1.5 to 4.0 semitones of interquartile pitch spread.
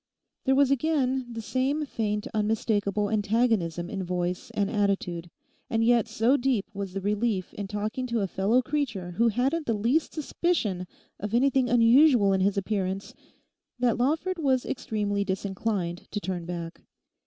No: average, 4.4 semitones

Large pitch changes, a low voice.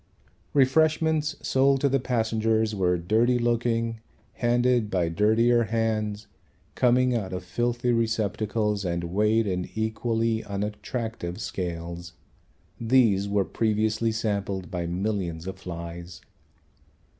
No: average, 3.8 semitones; low, 110 Hz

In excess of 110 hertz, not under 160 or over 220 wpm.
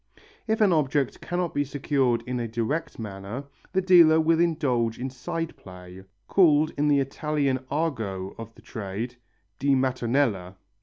No: low, 135 Hz; average, 150 wpm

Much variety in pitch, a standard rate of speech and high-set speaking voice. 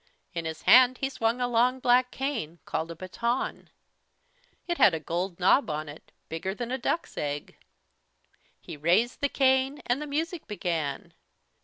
Yes: wide, 7.7 semitones; average, 165 wpm; high, 235 Hz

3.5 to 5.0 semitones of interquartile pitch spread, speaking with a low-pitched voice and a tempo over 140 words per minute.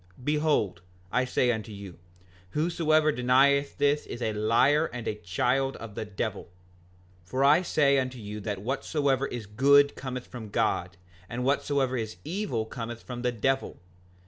Yes: average, 4.3 semitones; low, 125 Hz; average, 160 wpm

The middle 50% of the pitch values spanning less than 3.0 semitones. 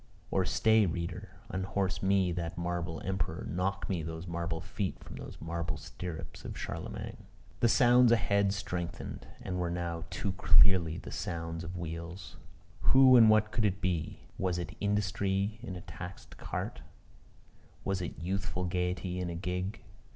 Yes: narrow, 2.6 semitones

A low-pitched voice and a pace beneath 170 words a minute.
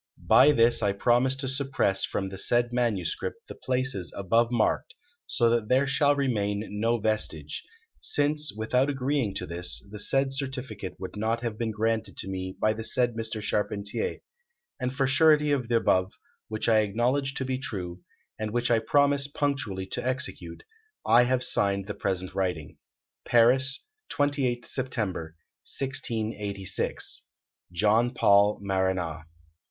Yes: low, 115 Hz; average, 145 wpm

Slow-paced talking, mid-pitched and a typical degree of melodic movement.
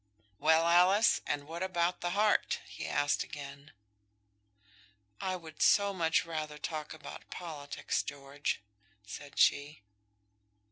Yes: slow, 120 wpm; medium, 160 Hz; average, 3.4 semitones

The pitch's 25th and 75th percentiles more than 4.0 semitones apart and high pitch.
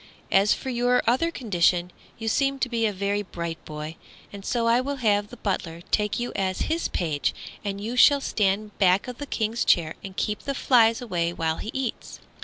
Yes: average, 4.7 semitones; high, 210 Hz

